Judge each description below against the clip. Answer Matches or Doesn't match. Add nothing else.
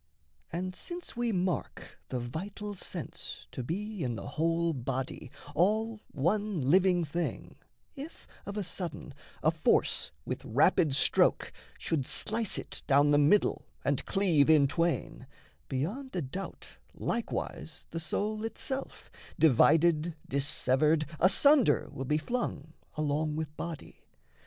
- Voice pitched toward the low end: Doesn't match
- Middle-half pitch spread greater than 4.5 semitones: Matches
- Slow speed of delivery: Matches